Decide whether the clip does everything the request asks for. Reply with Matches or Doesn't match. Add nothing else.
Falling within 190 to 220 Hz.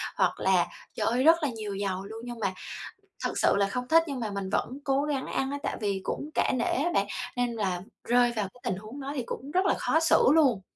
Doesn't match